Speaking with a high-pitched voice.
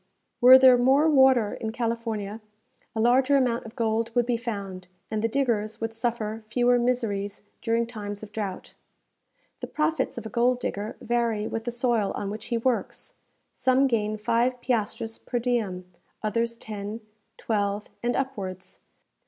Yes: high, 230 Hz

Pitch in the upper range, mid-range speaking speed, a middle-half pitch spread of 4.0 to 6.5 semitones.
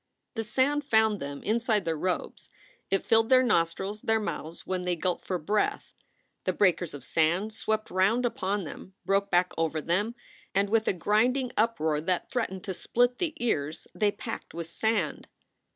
Yes: high, 200 Hz; average, 170 wpm; average, 4.6 semitones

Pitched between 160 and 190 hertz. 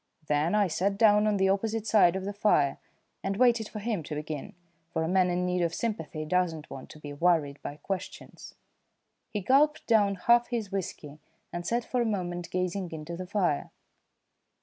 Yes: medium, 185 Hz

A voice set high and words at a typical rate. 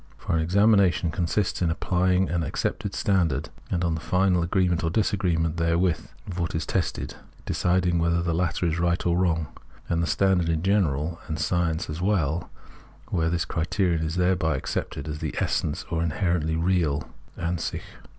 No: very low, 85 Hz; average, 170 wpm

